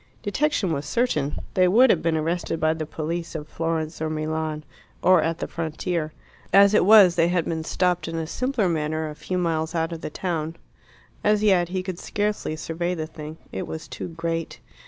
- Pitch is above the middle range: No, medium, 165 Hz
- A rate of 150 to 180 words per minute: No, average, 200 wpm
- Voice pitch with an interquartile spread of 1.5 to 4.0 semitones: Yes, narrow, 2.6 semitones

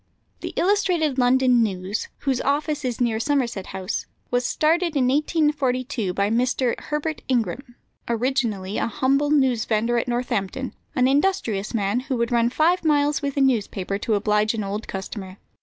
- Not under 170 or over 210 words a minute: No, average, 155 wpm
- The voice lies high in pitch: Yes, very high, 250 Hz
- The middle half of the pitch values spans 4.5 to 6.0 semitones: Yes, average, 4.8 semitones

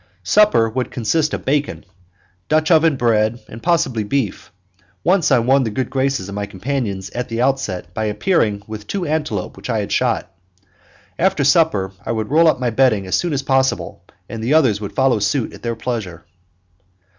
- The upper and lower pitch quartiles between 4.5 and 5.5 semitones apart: Yes, average, 5.1 semitones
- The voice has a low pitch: Yes, low, 125 Hz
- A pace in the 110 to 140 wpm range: No, average, 190 wpm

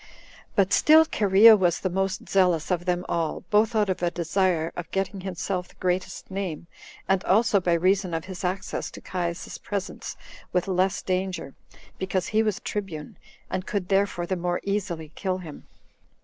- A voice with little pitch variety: Yes, narrow, 1.9 semitones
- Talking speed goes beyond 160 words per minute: Yes, average, 170 wpm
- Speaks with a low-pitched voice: No, medium, 185 Hz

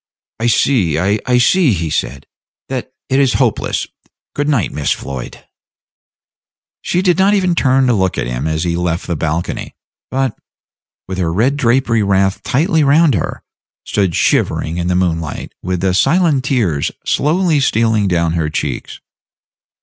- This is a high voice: No, low, 110 Hz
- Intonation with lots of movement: Yes, wide, 8.1 semitones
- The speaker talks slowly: No, average, 155 wpm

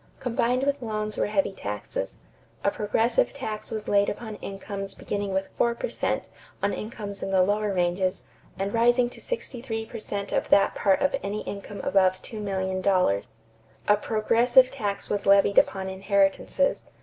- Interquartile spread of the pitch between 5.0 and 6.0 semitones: No, average, 2.8 semitones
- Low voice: No, high, 205 Hz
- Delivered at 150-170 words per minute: Yes, average, 160 wpm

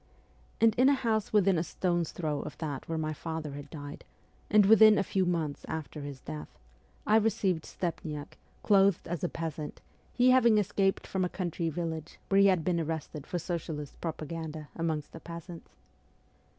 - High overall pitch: No, medium, 170 Hz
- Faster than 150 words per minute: Yes, average, 175 wpm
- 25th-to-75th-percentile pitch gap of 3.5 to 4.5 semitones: Yes, average, 4.0 semitones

